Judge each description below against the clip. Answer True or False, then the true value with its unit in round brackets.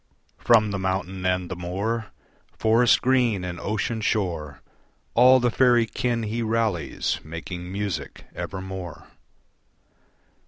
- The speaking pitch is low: True (100 Hz)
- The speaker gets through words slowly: True (115 wpm)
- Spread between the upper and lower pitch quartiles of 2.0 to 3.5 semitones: False (4.2 semitones)